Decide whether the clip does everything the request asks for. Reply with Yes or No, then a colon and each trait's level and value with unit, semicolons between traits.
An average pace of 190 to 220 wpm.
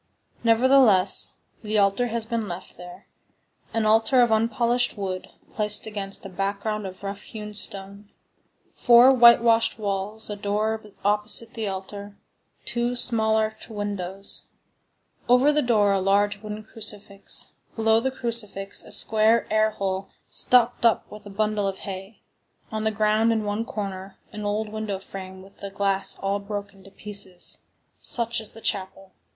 No: average, 145 wpm